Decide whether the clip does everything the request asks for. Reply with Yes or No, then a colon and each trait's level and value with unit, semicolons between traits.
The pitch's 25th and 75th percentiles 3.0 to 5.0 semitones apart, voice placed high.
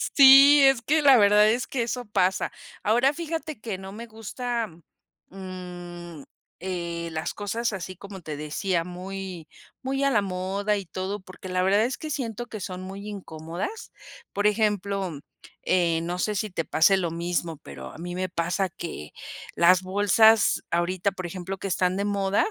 Yes: average, 3.5 semitones; high, 195 Hz